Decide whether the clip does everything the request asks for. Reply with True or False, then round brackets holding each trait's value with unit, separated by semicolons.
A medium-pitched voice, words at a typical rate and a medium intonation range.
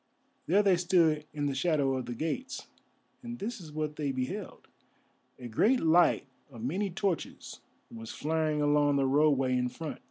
True (155 Hz; 165 wpm; 4.7 semitones)